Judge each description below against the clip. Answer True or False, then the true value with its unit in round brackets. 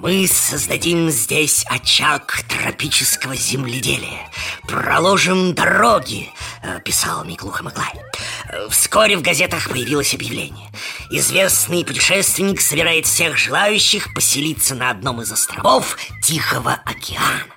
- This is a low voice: False (160 Hz)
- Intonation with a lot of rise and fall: True (6.2 semitones)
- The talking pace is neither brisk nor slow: False (95 wpm)